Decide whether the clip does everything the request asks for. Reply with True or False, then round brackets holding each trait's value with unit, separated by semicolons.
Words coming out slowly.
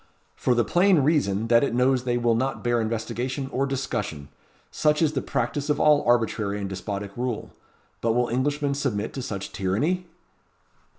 False (170 wpm)